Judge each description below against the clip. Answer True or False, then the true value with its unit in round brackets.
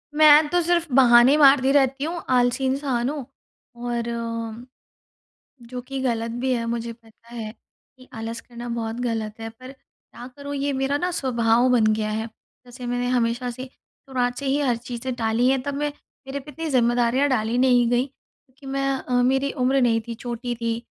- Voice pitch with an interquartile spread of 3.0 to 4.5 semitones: False (2.5 semitones)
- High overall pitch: True (250 Hz)